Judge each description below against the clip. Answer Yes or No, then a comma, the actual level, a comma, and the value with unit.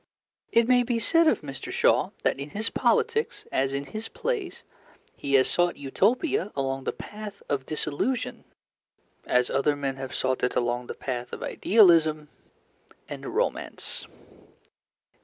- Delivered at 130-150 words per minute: Yes, average, 145 wpm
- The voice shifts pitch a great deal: Yes, wide, 8.9 semitones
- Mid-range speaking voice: Yes, medium, 150 Hz